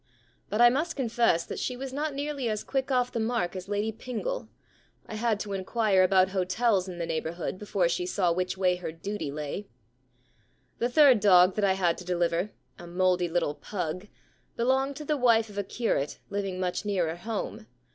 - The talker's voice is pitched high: Yes, high, 200 Hz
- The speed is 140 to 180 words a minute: No, average, 195 wpm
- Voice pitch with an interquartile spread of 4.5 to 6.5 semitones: Yes, average, 4.9 semitones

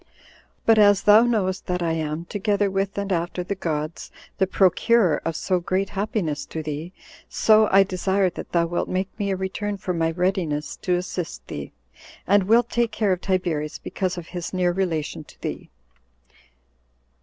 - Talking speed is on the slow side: No, average, 175 wpm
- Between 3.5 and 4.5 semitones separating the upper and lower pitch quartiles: No, average, 2.9 semitones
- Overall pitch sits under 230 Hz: Yes, medium, 185 Hz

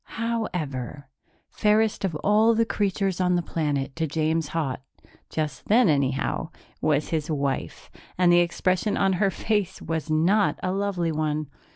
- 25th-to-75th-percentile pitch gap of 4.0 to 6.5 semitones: Yes, average, 4.7 semitones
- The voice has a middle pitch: Yes, medium, 170 Hz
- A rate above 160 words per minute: No, average, 150 wpm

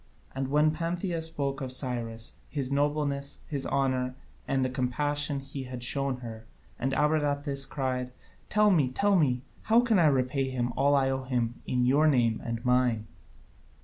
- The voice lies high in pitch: No, low, 135 Hz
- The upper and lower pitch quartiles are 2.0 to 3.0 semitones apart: Yes, narrow, 2.6 semitones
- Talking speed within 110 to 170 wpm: Yes, average, 165 wpm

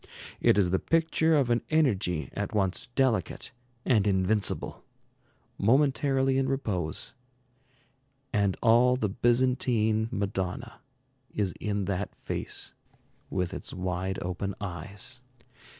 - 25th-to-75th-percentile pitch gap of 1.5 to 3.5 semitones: No, average, 5.0 semitones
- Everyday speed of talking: No, slow, 110 wpm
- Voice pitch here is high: No, low, 105 Hz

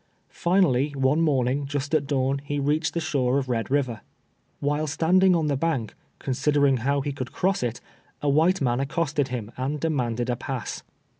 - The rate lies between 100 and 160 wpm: No, average, 180 wpm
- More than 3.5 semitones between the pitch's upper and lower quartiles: No, average, 2.9 semitones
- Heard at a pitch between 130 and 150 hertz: Yes, medium, 140 Hz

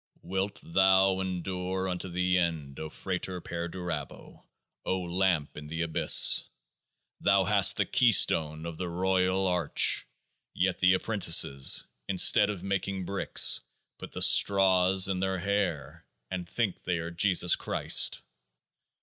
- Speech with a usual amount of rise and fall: No, narrow, 2.0 semitones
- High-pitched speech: No, very low, 90 Hz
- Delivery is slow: Yes, slow, 130 wpm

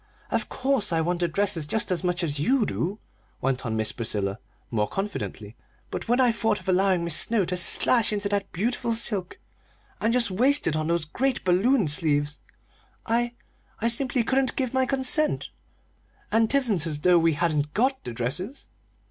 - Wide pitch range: Yes, wide, 6.9 semitones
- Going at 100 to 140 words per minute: No, average, 180 wpm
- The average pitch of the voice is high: Yes, high, 195 Hz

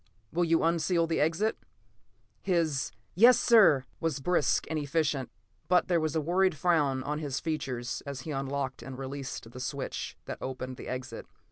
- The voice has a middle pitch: Yes, medium, 150 Hz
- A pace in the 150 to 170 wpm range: Yes, average, 165 wpm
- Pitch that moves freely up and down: No, average, 3.8 semitones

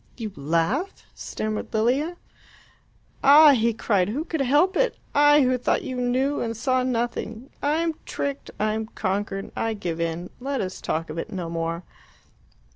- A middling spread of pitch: No, wide, 6.3 semitones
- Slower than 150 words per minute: No, average, 165 wpm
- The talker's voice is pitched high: Yes, high, 235 Hz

